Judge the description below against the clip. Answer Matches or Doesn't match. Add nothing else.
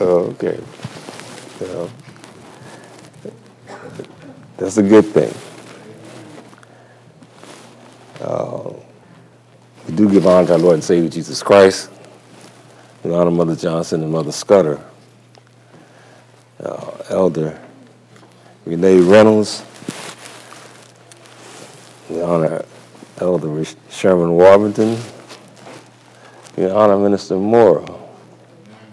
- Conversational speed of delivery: Doesn't match